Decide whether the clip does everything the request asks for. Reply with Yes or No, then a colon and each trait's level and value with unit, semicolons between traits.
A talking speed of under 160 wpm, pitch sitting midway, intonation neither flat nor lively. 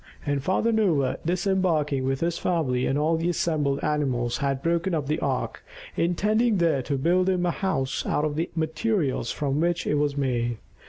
No: average, 180 wpm; medium, 155 Hz; average, 4.2 semitones